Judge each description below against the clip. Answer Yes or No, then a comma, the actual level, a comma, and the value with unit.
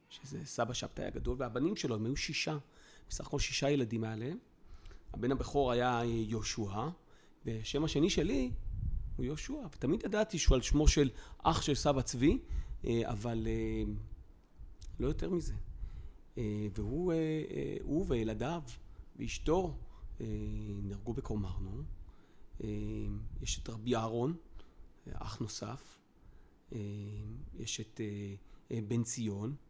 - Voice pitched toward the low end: Yes, low, 115 Hz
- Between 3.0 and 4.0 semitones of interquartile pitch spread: No, average, 4.5 semitones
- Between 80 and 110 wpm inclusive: Yes, average, 105 wpm